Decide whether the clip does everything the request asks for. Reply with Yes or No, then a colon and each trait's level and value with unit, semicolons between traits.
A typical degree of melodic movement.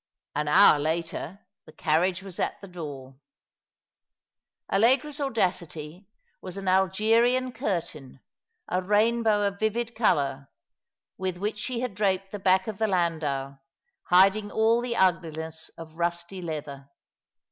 Yes: average, 4.9 semitones